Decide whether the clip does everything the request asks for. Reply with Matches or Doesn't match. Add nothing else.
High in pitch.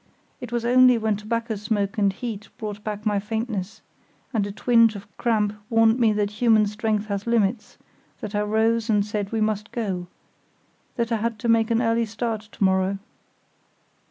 Matches